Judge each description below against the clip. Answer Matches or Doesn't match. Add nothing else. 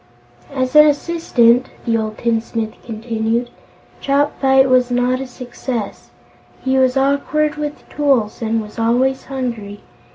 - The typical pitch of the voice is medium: Doesn't match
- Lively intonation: Doesn't match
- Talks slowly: Matches